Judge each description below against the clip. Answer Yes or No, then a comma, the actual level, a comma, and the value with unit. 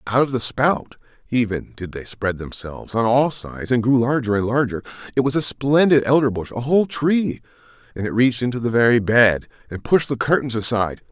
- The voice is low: Yes, low, 120 Hz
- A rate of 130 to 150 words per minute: No, average, 200 wpm